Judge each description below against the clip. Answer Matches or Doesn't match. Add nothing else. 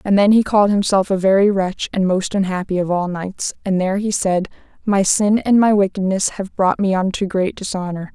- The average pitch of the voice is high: Matches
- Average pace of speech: Doesn't match